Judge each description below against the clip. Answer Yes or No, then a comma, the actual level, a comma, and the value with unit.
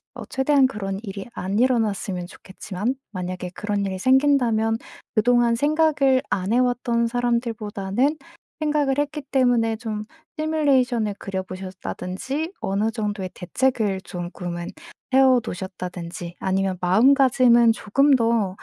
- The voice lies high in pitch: Yes, high, 225 Hz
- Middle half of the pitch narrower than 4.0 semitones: No, average, 5.3 semitones